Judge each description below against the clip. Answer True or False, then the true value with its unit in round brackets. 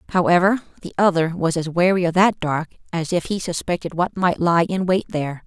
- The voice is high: False (175 Hz)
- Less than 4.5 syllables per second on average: False (5.7 syllables/s)